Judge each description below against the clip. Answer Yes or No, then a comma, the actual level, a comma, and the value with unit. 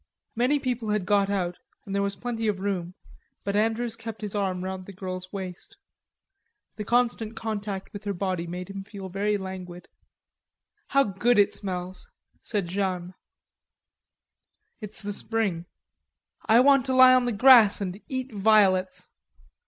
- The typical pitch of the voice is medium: No, high, 200 Hz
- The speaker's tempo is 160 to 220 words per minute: No, average, 150 wpm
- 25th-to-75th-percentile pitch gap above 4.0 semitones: No, average, 3.2 semitones